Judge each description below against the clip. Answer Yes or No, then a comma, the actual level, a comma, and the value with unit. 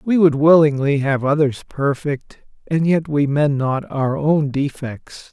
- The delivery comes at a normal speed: Yes, average, 160 wpm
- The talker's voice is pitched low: No, medium, 145 Hz